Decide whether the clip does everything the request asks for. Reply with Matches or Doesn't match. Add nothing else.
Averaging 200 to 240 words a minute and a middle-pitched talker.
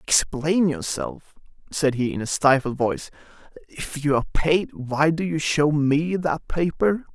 Doesn't match